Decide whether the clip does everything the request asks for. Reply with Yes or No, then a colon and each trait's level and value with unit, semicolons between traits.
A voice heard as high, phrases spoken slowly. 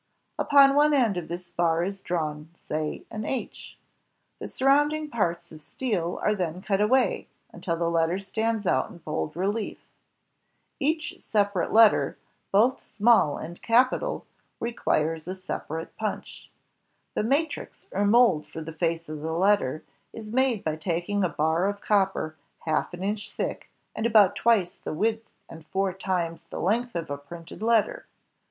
No: high, 195 Hz; average, 160 wpm